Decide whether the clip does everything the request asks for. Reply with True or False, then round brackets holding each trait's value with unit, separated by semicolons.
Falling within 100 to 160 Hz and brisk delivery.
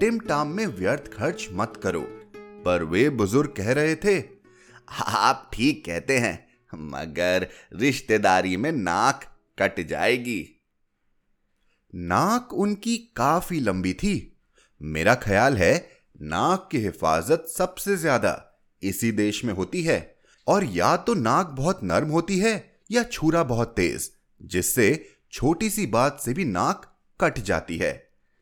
False (140 Hz; 130 wpm)